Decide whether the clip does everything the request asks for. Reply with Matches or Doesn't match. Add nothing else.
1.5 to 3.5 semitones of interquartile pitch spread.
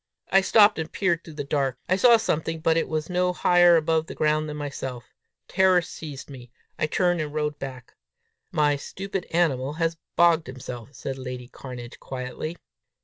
Doesn't match